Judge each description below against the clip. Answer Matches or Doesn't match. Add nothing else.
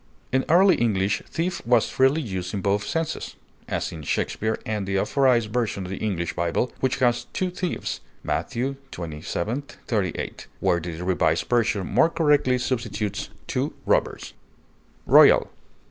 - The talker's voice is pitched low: Matches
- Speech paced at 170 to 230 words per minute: Doesn't match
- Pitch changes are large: Matches